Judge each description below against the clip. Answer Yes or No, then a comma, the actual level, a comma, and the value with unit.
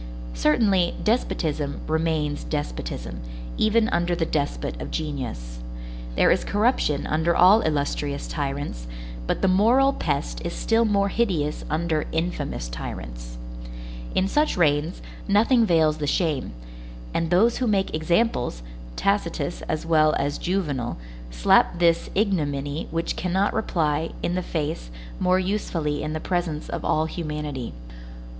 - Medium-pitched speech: Yes, medium, 160 Hz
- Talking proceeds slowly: Yes, slow, 130 wpm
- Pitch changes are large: No, average, 4.4 semitones